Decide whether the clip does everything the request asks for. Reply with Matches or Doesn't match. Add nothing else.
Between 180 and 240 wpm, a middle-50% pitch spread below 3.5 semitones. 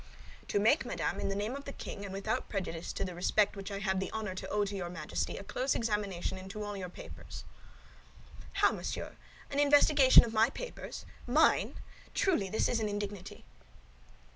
Matches